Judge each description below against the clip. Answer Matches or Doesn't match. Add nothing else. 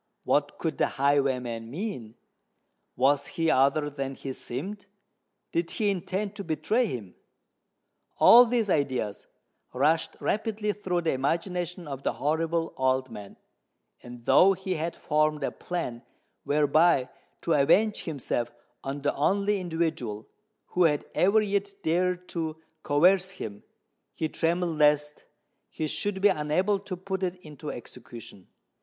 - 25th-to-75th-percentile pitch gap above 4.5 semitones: Matches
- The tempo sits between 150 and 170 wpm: Doesn't match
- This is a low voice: Doesn't match